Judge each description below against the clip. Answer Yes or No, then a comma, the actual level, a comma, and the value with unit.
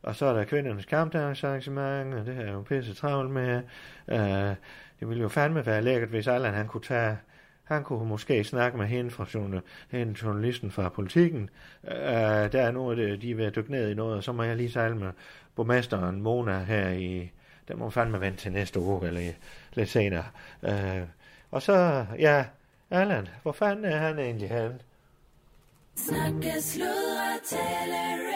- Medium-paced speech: Yes, average, 180 wpm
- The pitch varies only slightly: No, average, 4.9 semitones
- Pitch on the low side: Yes, low, 115 Hz